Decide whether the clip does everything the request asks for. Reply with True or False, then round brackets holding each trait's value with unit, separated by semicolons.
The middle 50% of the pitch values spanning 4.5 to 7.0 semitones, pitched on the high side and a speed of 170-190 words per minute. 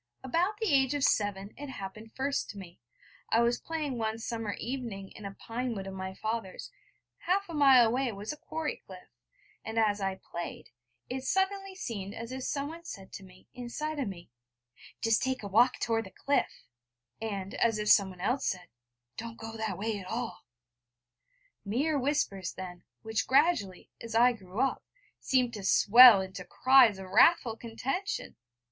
True (5.1 semitones; 230 Hz; 175 wpm)